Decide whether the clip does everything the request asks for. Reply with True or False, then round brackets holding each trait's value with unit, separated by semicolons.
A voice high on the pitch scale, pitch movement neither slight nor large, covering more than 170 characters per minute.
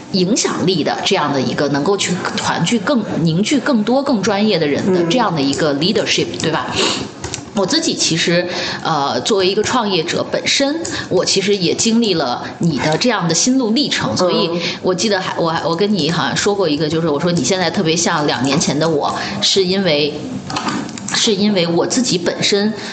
True (195 Hz; 4.7 semitones; 300 characters per minute)